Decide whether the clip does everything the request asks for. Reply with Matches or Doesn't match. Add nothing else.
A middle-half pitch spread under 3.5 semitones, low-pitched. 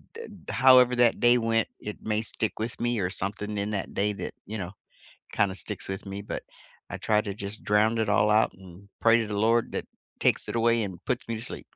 Matches